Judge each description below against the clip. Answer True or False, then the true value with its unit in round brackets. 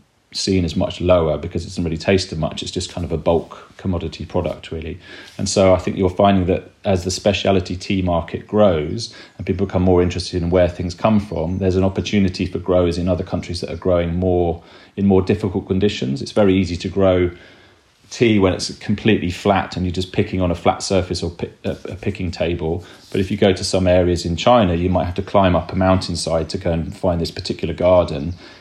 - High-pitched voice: False (90 Hz)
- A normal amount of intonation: False (1.9 semitones)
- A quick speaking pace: True (220 wpm)